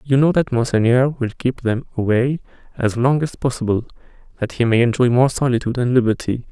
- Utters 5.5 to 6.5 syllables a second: Yes, 5.8 syllables/s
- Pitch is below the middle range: Yes, low, 125 Hz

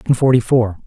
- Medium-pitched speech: No, low, 120 Hz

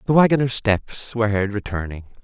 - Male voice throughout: Yes, male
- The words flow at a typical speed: Yes, average, 160 wpm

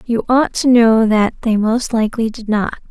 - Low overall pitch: No, high, 225 Hz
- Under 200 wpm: No, fast, 205 wpm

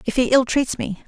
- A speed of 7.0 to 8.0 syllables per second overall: No, 5.8 syllables/s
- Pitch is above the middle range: Yes, very high, 250 Hz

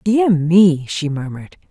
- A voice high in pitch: No, medium, 170 Hz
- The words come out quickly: No, average, 140 wpm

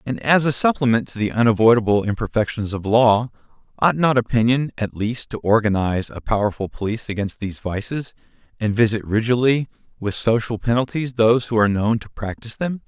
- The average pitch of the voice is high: No, low, 115 Hz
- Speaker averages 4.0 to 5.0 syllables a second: No, 5.9 syllables/s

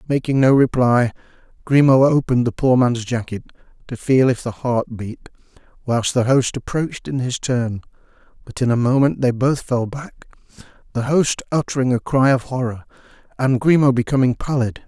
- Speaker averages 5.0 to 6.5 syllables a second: Yes, 5.1 syllables/s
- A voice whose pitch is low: Yes, low, 125 Hz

